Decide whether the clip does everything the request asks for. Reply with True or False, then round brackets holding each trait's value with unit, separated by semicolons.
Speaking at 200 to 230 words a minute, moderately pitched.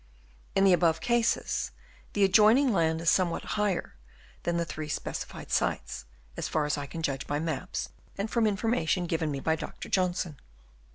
False (175 wpm; 170 Hz)